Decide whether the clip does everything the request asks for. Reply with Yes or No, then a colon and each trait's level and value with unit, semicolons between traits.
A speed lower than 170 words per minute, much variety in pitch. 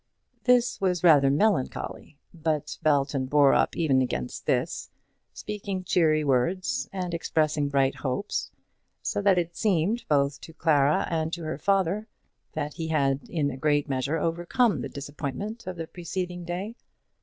No: average, 150 wpm; average, 4.4 semitones